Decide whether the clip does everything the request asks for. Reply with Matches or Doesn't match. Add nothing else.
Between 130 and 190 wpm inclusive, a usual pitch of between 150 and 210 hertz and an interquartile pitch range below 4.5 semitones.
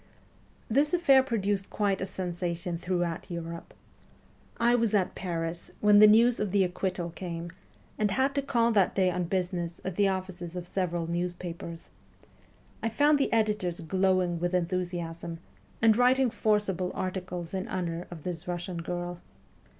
Matches